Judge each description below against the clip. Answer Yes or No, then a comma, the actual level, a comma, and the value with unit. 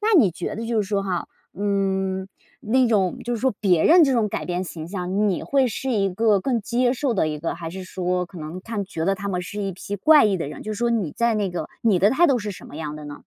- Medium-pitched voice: No, high, 200 Hz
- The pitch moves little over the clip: No, average, 4.2 semitones